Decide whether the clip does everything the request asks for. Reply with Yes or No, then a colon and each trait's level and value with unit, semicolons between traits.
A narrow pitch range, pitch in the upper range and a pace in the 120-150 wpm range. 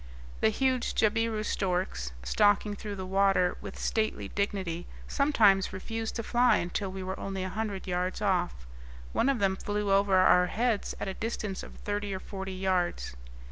No: narrow, 2.3 semitones; high, 195 Hz; average, 170 wpm